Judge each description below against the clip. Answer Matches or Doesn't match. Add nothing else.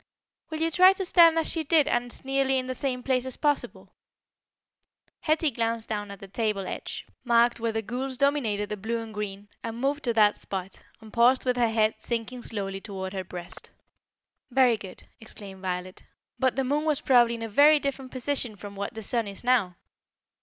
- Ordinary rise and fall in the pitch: Matches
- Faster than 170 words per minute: Matches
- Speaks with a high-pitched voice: Matches